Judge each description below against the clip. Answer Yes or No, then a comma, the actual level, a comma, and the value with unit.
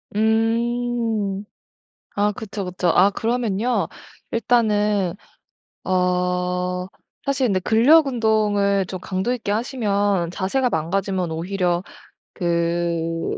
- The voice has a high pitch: Yes, high, 200 Hz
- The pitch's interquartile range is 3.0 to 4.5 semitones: Yes, average, 3.8 semitones